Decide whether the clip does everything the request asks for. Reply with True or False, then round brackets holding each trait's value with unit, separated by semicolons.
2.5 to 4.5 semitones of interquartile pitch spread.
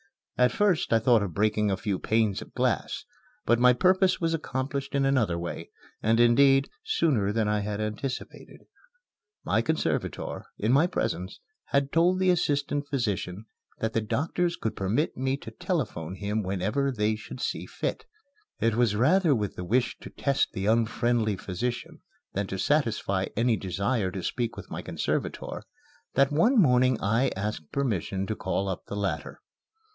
False (5.2 semitones)